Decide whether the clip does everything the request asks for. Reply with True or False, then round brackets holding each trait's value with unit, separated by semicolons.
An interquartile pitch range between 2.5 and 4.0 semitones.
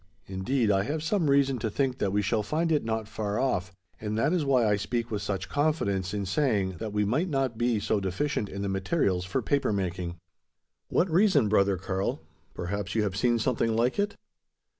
False (5.5 semitones)